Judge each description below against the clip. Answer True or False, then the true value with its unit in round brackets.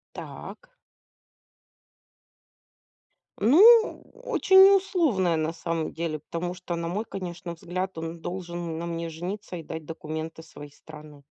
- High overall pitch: False (170 Hz)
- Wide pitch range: False (2.8 semitones)